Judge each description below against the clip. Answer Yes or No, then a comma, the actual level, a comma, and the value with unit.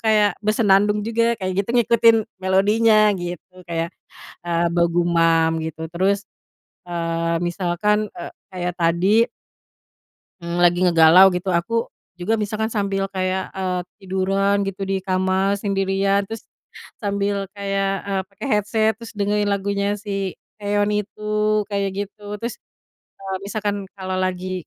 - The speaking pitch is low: No, high, 195 Hz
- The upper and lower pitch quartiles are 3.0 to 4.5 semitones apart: No, narrow, 2.4 semitones